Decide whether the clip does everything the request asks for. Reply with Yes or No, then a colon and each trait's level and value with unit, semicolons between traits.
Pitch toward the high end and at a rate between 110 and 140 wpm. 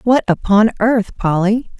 Yes: high, 215 Hz; slow, 135 wpm